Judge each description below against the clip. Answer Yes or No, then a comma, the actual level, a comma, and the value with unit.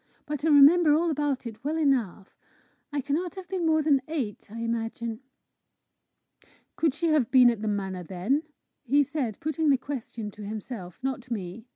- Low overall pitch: No, very high, 265 Hz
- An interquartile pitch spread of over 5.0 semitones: Yes, wide, 5.5 semitones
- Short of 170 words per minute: No, average, 175 wpm